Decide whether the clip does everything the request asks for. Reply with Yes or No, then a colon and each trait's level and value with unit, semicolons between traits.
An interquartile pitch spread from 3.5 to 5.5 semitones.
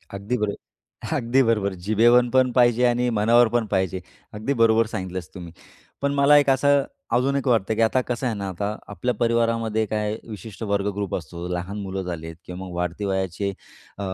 Yes: average, 4.1 semitones